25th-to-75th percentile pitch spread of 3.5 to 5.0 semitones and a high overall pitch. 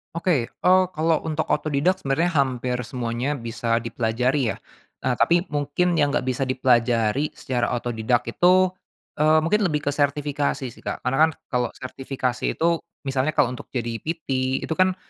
No: average, 4.2 semitones; low, 135 Hz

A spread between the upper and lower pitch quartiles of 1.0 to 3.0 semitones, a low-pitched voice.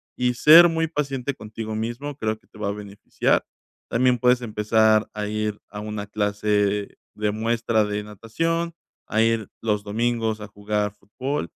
Yes: average, 2.7 semitones; low, 110 Hz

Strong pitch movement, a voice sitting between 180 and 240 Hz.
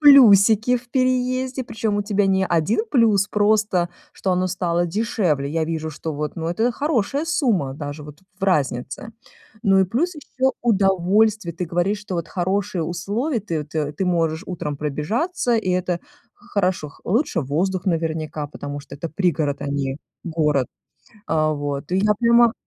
Yes: wide, 5.8 semitones; medium, 185 Hz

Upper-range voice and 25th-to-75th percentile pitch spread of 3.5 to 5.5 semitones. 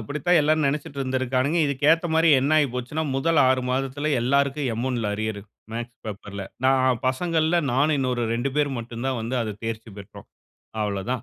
No: low, 130 Hz; average, 3.8 semitones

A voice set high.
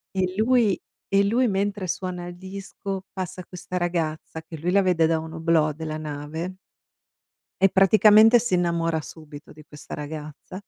No: medium, 175 Hz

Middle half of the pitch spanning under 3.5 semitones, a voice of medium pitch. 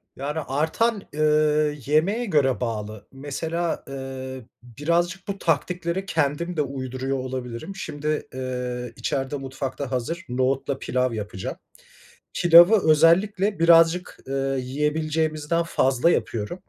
No: average, 4.3 semitones; medium, 145 Hz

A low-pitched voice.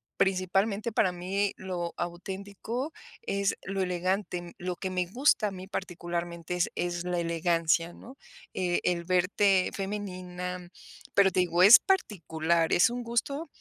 No: medium, 185 Hz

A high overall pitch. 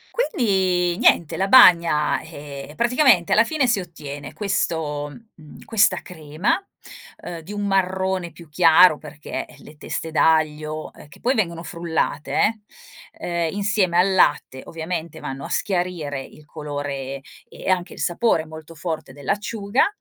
No: medium, 170 Hz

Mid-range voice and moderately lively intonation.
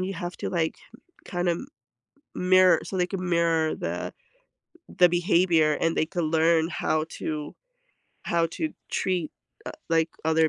No: medium, 170 Hz; narrow, 2.0 semitones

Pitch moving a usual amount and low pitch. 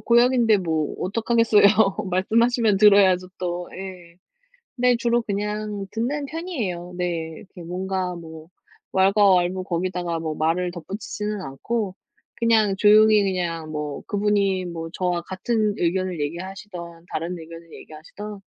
No: average, 3.5 semitones; high, 190 Hz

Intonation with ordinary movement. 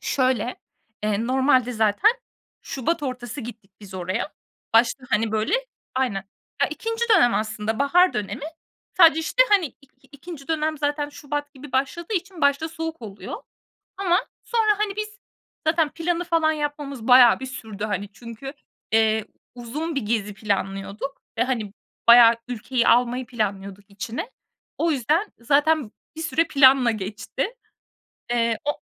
No: wide, 6.1 semitones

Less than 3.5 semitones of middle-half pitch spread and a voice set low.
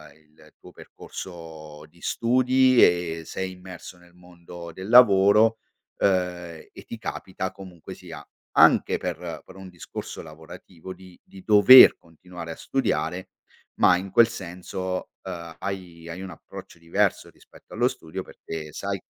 Yes: average, 2.7 semitones; very low, 90 Hz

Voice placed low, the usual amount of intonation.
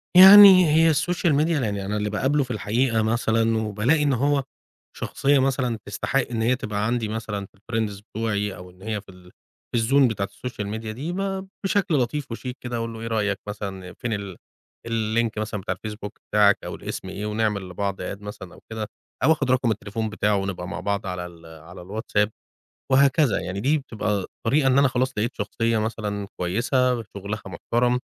Yes: low, 110 Hz; average, 4.0 semitones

